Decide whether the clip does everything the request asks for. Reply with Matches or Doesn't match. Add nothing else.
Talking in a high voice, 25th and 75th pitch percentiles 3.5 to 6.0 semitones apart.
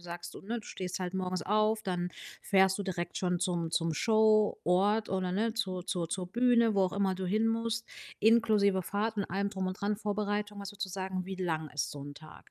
Doesn't match